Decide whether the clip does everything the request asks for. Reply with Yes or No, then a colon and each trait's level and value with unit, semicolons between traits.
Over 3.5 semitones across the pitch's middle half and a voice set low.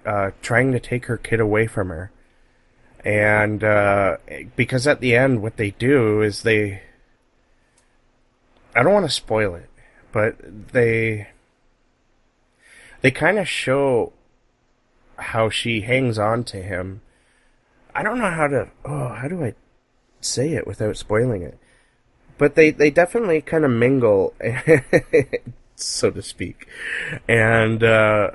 Yes: average, 4.0 semitones; low, 115 Hz